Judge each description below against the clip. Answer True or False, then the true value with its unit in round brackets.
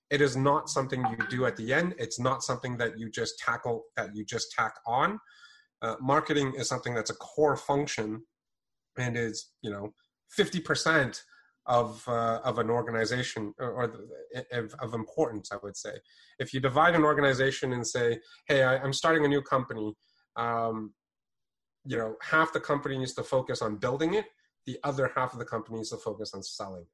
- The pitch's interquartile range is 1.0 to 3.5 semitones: False (4.0 semitones)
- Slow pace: False (190 wpm)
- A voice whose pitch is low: True (130 Hz)